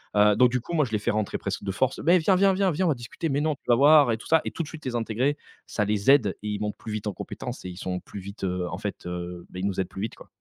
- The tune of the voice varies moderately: No, wide, 6.6 semitones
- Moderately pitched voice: No, low, 115 Hz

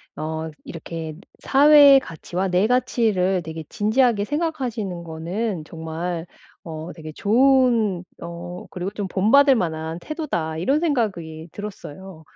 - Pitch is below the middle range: No, medium, 185 Hz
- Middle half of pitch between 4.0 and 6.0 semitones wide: No, wide, 6.9 semitones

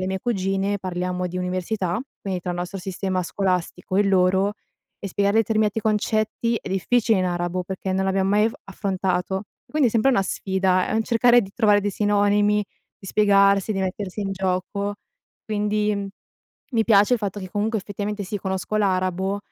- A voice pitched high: Yes, high, 195 Hz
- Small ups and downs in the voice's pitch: Yes, narrow, 2.0 semitones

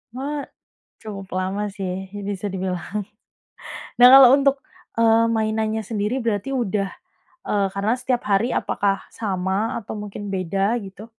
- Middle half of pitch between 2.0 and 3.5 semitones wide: Yes, average, 3.0 semitones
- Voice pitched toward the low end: No, high, 210 Hz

